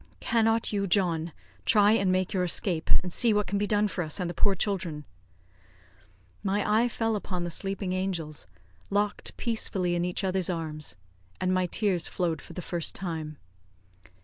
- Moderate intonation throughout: Yes, average, 3.0 semitones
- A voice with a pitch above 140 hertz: Yes, medium, 185 Hz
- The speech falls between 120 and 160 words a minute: No, average, 175 wpm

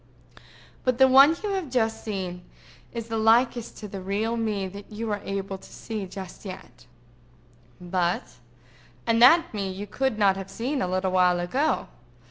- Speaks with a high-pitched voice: Yes, high, 200 Hz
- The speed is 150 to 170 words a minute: Yes, average, 165 wpm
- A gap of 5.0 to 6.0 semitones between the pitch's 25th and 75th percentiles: No, average, 4.0 semitones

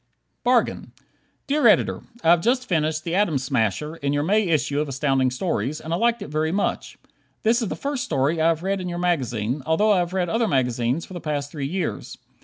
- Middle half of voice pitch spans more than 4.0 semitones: Yes, average, 5.3 semitones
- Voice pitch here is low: No, medium, 160 Hz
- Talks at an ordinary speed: No, fast, 215 wpm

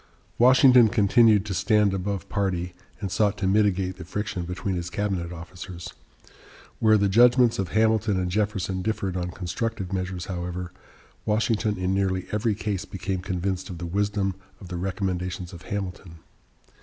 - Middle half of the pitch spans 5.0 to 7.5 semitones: No, average, 2.7 semitones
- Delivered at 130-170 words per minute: Yes, average, 155 wpm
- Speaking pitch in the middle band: No, very low, 95 Hz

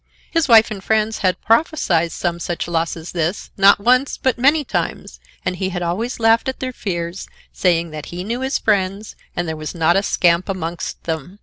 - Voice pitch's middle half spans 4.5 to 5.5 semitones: Yes, average, 4.8 semitones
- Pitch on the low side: No, high, 190 Hz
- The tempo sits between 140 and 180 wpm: No, average, 200 wpm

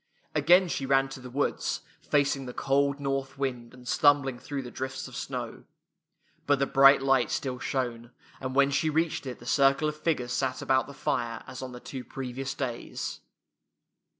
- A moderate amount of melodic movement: No, narrow, 1.7 semitones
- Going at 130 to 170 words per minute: No, average, 185 wpm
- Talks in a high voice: No, low, 135 Hz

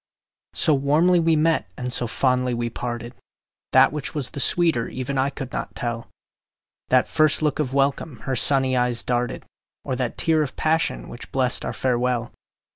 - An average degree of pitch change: Yes, average, 3.5 semitones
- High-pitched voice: No, low, 130 Hz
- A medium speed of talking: Yes, average, 175 wpm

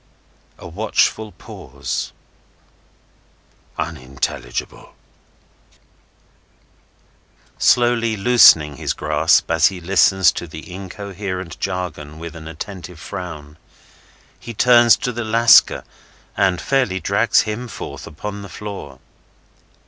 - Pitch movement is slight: No, average, 5.0 semitones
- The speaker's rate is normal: No, slow, 95 wpm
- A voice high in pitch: No, very low, 95 Hz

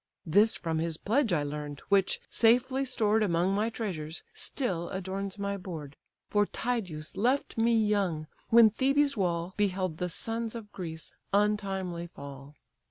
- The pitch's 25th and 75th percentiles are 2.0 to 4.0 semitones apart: No, average, 4.9 semitones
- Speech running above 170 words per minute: No, average, 145 wpm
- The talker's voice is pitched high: Yes, high, 195 Hz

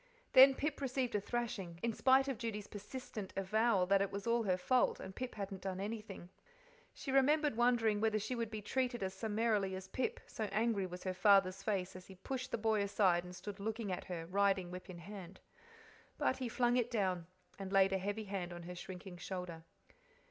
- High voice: Yes, high, 205 Hz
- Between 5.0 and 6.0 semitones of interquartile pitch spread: No, average, 3.8 semitones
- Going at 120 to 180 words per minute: No, fast, 205 wpm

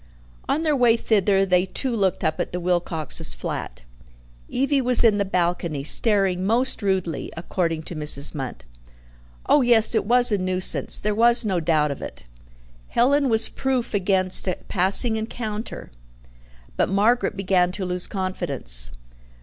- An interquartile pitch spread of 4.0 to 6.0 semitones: Yes, average, 4.6 semitones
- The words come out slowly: No, average, 150 wpm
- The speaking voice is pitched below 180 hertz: No, high, 195 Hz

